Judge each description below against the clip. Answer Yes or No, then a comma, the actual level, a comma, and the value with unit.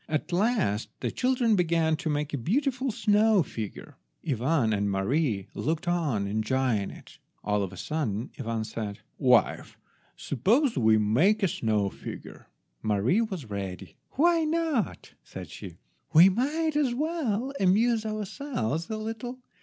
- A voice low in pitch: No, medium, 165 Hz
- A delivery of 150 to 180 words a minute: No, average, 140 wpm